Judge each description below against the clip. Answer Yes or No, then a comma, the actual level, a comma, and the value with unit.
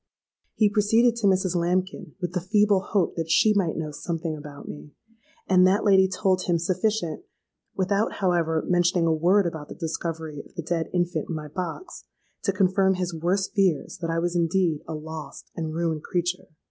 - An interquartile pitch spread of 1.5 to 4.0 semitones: Yes, average, 2.8 semitones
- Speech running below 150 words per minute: No, average, 185 wpm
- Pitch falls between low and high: Yes, medium, 175 Hz